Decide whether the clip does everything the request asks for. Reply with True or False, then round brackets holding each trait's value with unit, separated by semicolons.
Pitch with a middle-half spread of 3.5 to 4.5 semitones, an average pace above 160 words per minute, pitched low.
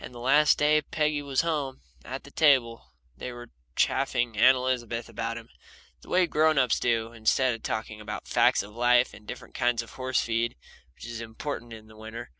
False (2.8 semitones; 200 wpm; 120 Hz)